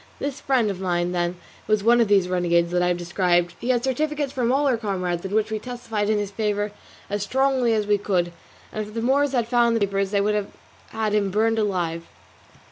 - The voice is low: No, high, 210 Hz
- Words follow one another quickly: Yes, fast, 220 wpm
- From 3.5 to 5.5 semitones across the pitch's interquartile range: Yes, average, 4.3 semitones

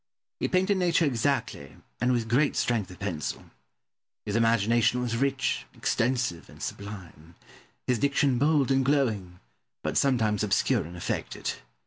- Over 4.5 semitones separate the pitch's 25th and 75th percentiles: Yes, average, 5.1 semitones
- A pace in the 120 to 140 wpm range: Yes, slow, 135 wpm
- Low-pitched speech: Yes, low, 120 Hz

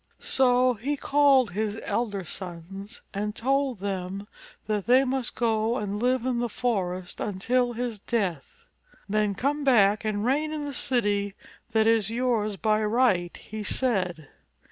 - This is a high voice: Yes, high, 220 Hz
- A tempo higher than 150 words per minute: No, average, 145 wpm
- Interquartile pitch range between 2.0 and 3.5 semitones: No, average, 3.9 semitones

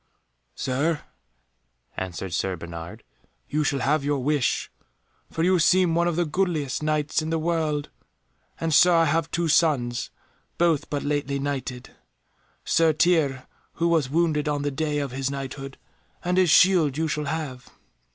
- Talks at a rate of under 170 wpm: Yes, average, 155 wpm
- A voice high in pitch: No, medium, 150 Hz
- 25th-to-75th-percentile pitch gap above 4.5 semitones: No, average, 3.1 semitones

